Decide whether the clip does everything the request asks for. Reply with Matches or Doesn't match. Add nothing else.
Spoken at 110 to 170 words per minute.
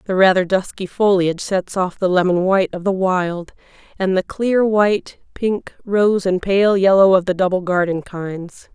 Doesn't match